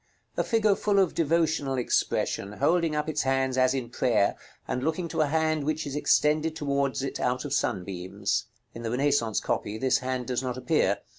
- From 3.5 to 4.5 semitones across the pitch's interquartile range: Yes, average, 4.0 semitones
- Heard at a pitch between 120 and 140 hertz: Yes, low, 135 Hz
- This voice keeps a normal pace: Yes, average, 190 wpm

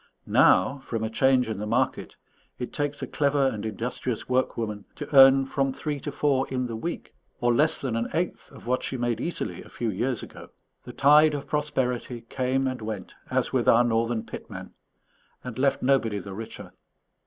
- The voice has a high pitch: No, low, 125 Hz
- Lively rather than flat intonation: No, average, 3.3 semitones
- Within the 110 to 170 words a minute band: No, average, 190 wpm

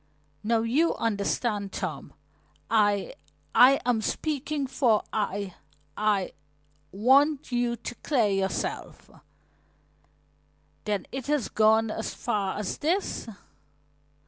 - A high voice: Yes, high, 225 Hz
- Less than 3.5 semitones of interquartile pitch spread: No, average, 4.3 semitones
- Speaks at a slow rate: Yes, slow, 100 wpm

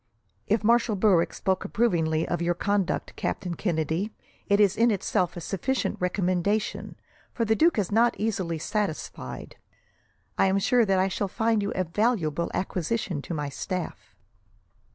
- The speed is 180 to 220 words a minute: No, average, 155 wpm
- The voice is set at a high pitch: Yes, high, 195 Hz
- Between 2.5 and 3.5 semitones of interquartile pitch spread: No, average, 4.0 semitones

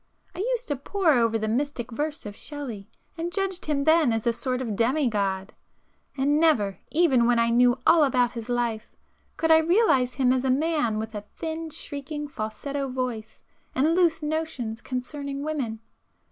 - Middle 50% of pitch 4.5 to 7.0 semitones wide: Yes, average, 5.1 semitones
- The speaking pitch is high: Yes, very high, 265 Hz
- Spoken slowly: No, average, 175 wpm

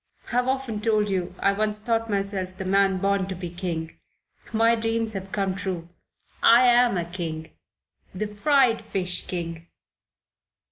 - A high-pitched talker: Yes, high, 200 Hz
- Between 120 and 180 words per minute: Yes, average, 150 wpm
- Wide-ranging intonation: No, average, 3.6 semitones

